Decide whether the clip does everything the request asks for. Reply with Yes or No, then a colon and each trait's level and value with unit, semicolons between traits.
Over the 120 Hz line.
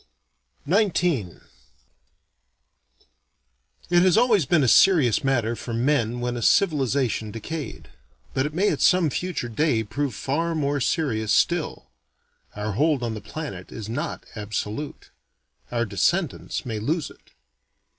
Yes: low, 135 Hz